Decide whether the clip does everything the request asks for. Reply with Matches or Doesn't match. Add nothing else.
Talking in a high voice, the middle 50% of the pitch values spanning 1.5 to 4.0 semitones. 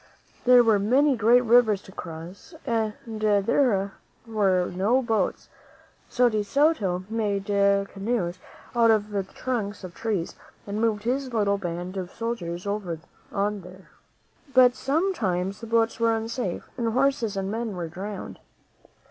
Matches